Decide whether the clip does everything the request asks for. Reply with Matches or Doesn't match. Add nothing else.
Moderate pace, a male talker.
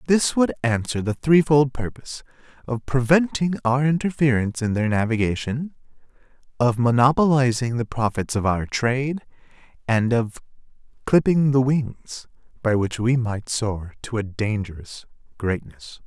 Doesn't match